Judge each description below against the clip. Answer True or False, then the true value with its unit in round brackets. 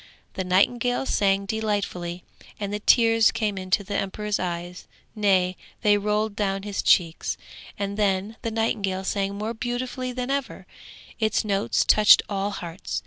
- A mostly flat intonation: True (2.2 semitones)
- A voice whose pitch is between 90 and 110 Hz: False (205 Hz)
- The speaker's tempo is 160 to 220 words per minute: False (145 wpm)